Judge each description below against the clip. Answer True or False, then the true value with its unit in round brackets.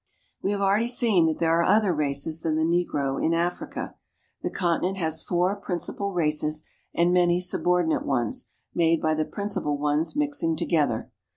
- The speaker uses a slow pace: False (165 wpm)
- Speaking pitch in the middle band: True (170 Hz)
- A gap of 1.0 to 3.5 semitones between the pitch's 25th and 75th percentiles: True (2.9 semitones)